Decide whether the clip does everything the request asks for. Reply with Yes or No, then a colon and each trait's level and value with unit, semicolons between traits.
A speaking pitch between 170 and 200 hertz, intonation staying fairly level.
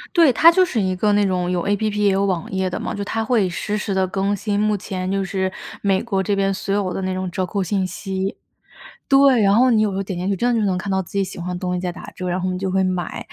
Yes: high, 195 Hz; narrow, 2.0 semitones